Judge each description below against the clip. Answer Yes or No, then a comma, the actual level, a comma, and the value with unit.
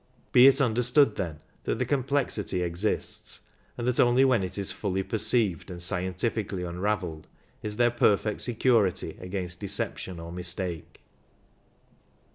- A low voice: Yes, low, 100 Hz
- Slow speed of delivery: Yes, slow, 130 wpm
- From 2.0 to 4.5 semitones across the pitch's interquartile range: No, average, 5.0 semitones